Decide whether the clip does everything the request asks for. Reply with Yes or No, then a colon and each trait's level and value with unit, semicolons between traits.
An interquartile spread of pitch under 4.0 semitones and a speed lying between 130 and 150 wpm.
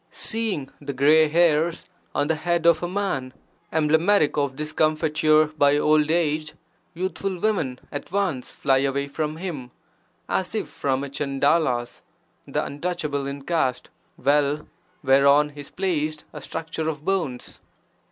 Yes: average, 2.9 semitones; slow, 135 wpm